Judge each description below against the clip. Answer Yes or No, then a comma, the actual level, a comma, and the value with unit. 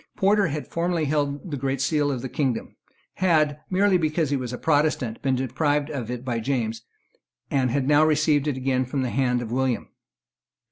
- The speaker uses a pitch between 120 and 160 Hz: Yes, medium, 140 Hz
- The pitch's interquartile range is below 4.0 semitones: Yes, average, 3.2 semitones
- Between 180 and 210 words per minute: Yes, average, 190 wpm